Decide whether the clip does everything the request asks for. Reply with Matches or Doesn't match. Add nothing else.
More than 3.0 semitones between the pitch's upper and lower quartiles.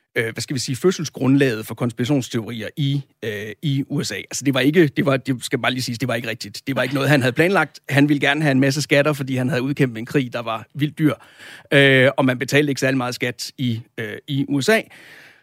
Doesn't match